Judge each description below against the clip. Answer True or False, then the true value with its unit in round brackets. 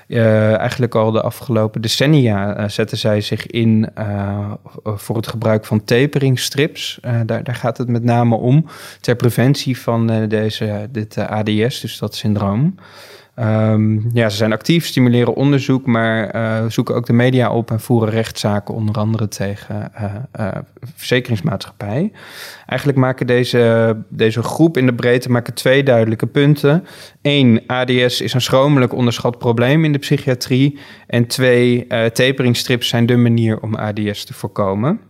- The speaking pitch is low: True (120 Hz)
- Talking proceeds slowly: False (155 wpm)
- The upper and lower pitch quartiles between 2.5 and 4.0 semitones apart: True (2.9 semitones)